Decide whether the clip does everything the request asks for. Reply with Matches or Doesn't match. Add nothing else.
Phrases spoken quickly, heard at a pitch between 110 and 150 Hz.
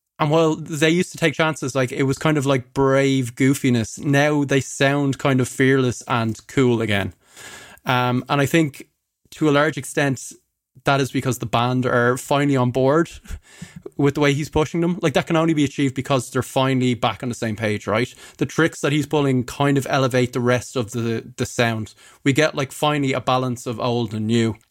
Matches